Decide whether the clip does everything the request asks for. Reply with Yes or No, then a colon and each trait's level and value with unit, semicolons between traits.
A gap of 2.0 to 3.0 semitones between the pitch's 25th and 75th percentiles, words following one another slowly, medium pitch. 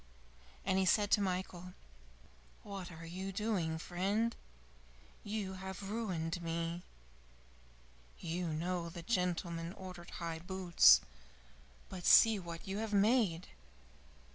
Yes: average, 2.7 semitones; slow, 115 wpm; medium, 180 Hz